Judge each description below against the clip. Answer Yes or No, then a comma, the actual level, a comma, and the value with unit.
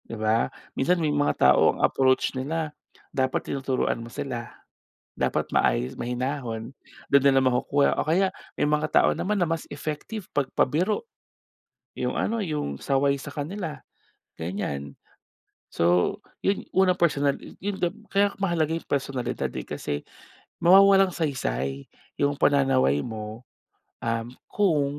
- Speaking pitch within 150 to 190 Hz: No, medium, 140 Hz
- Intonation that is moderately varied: No, wide, 5.9 semitones